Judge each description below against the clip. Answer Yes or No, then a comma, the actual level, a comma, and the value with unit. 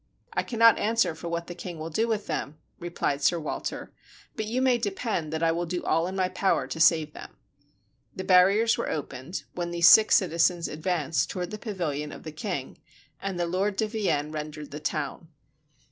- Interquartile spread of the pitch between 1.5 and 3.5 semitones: No, average, 4.2 semitones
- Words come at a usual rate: Yes, average, 195 wpm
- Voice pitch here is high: No, medium, 175 Hz